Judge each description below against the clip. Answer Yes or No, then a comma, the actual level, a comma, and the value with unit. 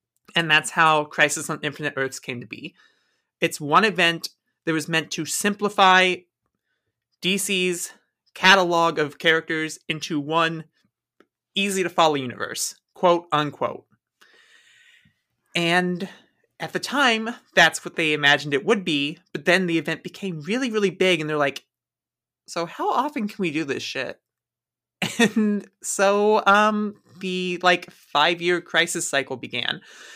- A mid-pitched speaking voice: Yes, medium, 170 Hz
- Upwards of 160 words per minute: No, average, 140 wpm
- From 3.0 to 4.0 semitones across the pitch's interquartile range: Yes, average, 3.7 semitones